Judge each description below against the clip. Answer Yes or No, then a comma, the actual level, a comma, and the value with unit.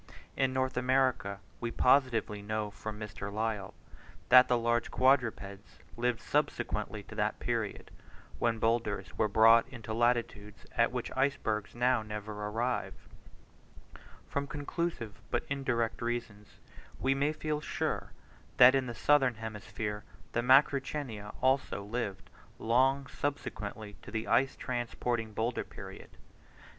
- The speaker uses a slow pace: Yes, slow, 125 wpm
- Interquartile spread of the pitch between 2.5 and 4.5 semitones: Yes, average, 3.4 semitones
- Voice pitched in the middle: No, low, 120 Hz